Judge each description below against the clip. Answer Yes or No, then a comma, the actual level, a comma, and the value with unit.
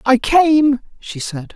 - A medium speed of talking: Yes, average, 155 wpm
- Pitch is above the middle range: Yes, very high, 260 Hz